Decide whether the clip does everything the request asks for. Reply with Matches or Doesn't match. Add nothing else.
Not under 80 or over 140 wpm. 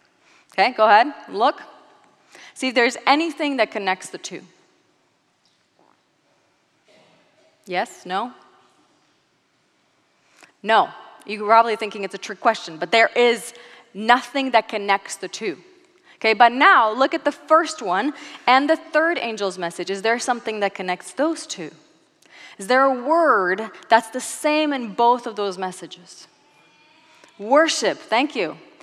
Matches